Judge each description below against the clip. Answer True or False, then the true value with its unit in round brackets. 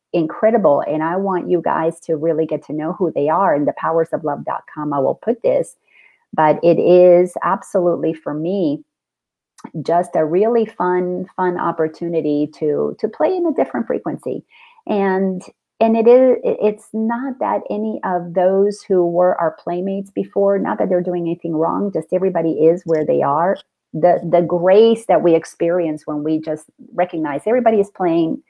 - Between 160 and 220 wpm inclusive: True (175 wpm)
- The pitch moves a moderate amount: True (4.7 semitones)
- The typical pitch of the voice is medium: True (180 Hz)